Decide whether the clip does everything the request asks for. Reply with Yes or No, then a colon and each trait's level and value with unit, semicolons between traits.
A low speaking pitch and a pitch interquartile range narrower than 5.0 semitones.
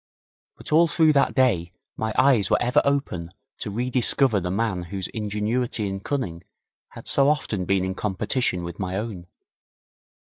No: low, 105 Hz; wide, 5.6 semitones